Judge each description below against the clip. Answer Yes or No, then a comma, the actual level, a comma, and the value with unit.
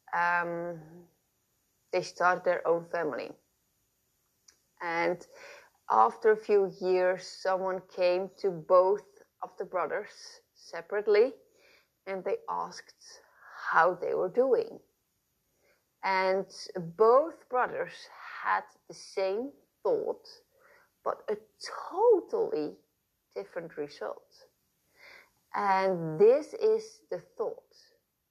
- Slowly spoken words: Yes, slow, 90 wpm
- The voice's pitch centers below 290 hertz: No, very high, 330 Hz